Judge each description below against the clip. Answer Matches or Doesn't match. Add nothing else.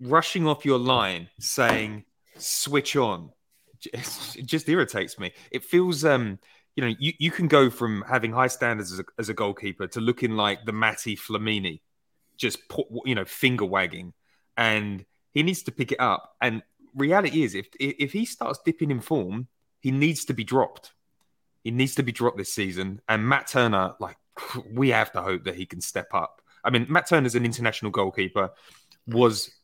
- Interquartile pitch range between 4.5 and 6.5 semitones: Matches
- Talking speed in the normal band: Matches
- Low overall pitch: Matches